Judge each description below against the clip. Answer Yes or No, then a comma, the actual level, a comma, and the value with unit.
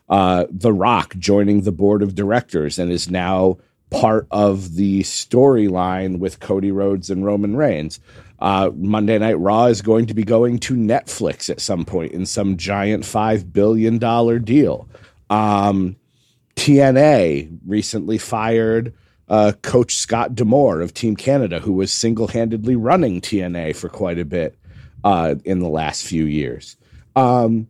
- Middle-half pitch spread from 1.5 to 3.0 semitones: No, average, 3.4 semitones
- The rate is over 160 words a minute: No, average, 150 wpm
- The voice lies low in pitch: Yes, low, 105 Hz